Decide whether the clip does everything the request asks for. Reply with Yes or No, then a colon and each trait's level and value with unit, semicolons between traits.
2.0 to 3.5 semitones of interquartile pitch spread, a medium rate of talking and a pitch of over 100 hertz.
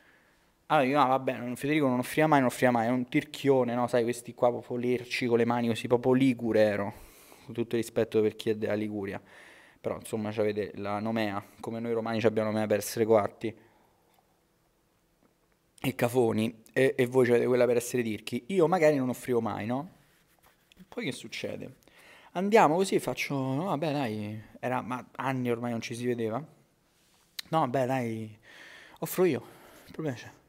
No: average, 2.9 semitones; fast, 180 wpm; low, 120 Hz